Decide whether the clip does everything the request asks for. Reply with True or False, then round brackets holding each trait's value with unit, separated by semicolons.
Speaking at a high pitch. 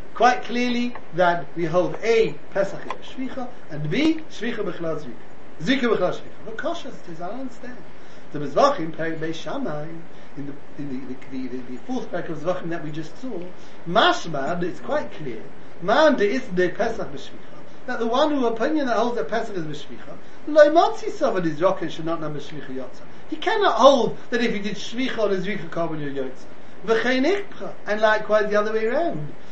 True (210 Hz)